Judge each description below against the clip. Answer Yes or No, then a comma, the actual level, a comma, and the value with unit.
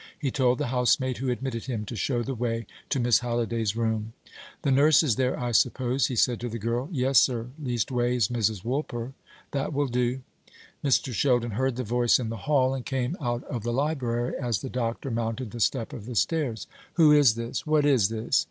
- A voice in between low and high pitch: No, low, 125 Hz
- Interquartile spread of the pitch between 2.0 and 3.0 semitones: Yes, narrow, 2.4 semitones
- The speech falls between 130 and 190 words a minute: No, fast, 205 wpm